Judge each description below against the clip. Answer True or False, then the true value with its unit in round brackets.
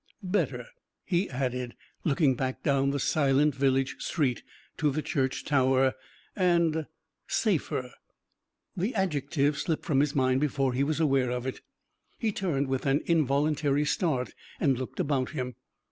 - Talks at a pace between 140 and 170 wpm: True (145 wpm)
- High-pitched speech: False (140 Hz)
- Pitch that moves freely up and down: False (2.9 semitones)